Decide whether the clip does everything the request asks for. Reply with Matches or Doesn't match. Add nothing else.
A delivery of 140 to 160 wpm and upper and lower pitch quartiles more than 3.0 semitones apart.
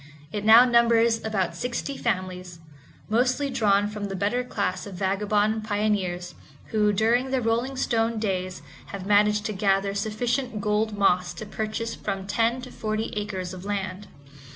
Doesn't match